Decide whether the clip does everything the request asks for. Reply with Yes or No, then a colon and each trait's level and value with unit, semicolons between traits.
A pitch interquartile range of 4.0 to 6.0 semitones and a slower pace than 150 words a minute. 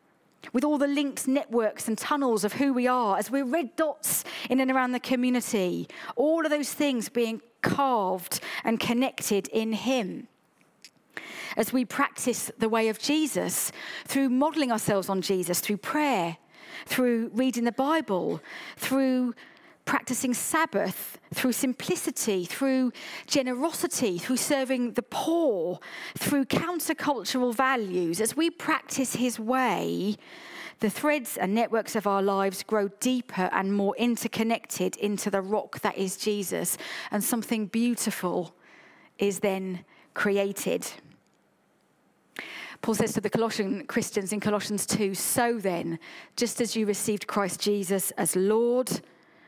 Yes: average, 4.3 semitones; slow, 135 wpm